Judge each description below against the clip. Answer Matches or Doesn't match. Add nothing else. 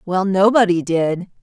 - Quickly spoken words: Doesn't match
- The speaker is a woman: Matches